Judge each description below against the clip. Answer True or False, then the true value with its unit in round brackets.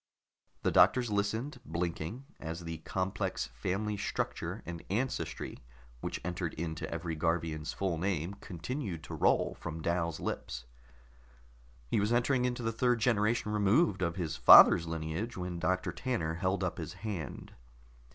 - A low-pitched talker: True (90 Hz)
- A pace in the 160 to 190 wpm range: False (140 wpm)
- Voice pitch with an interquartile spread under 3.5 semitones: False (4.6 semitones)